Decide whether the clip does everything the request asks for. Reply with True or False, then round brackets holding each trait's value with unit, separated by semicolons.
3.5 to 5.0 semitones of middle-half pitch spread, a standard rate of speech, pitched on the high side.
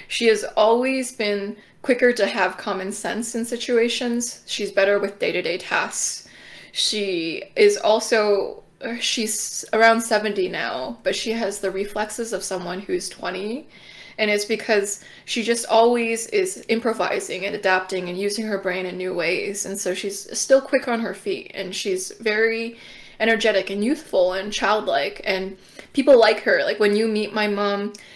False (2.8 semitones; 160 wpm; 215 Hz)